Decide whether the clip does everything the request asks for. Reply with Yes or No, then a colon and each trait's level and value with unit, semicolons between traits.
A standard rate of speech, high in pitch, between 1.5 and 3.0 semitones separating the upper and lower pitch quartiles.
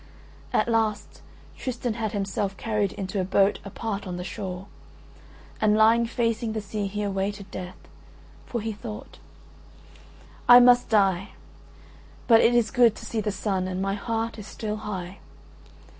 Yes: average, 155 wpm; high, 210 Hz; narrow, 2.6 semitones